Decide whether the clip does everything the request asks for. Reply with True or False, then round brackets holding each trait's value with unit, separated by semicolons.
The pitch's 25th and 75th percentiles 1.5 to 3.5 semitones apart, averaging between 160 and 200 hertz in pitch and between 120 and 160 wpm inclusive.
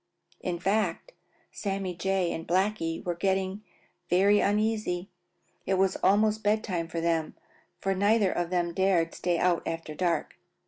True (2.7 semitones; 185 Hz; 145 wpm)